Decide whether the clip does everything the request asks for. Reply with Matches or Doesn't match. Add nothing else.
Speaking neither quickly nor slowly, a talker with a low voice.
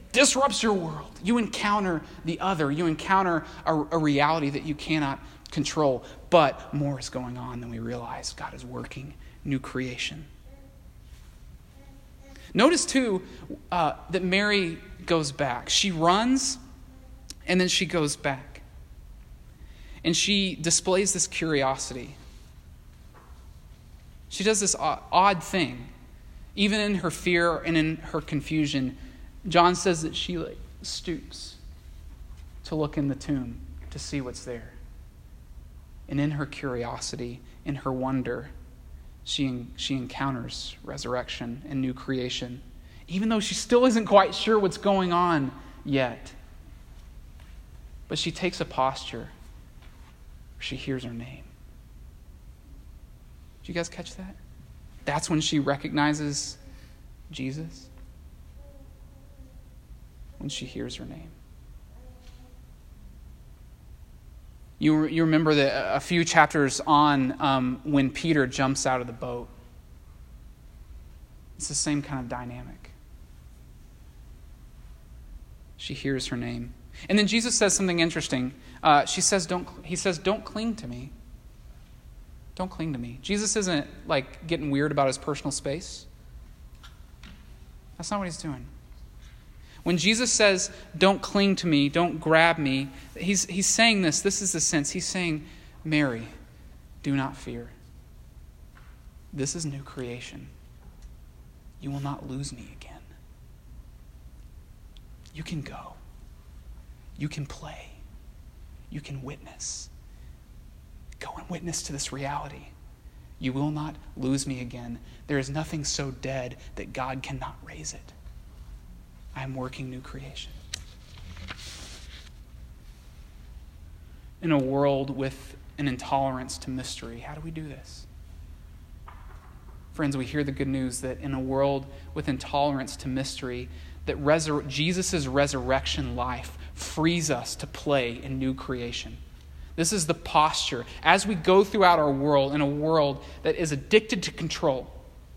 Doesn't match